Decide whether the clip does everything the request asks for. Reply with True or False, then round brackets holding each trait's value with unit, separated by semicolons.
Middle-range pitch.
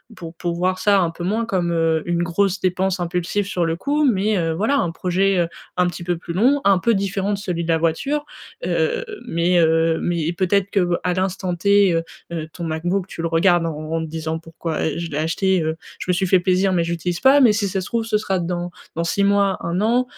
True (180 Hz)